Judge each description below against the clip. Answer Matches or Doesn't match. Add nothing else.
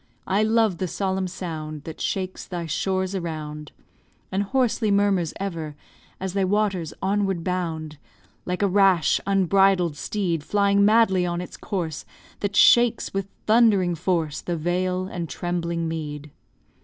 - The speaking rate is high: Doesn't match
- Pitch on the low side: Doesn't match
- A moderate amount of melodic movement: Matches